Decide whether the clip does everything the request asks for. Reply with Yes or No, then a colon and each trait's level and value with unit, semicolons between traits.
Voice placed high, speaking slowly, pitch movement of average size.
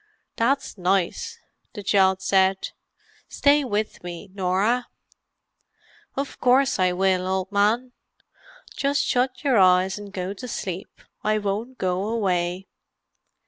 Yes: high, 200 Hz; slow, 120 wpm; average, 4.8 semitones